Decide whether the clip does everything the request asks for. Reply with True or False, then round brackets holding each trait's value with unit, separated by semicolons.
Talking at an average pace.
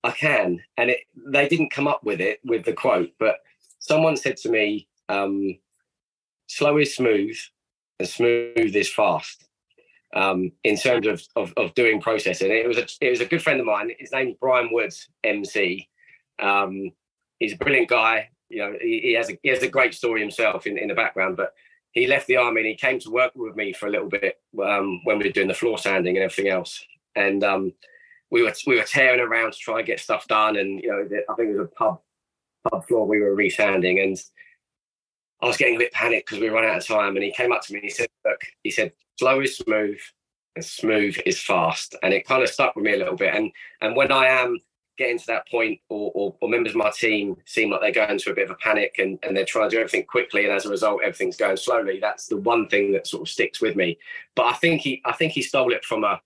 False (245 wpm)